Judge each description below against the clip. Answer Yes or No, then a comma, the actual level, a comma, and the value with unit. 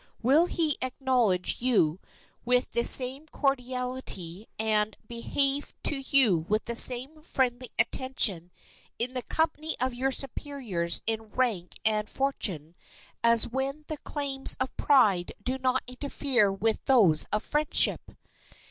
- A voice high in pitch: Yes, very high, 250 Hz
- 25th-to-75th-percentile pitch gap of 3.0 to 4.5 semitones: Yes, average, 4.1 semitones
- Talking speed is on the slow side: Yes, slow, 130 wpm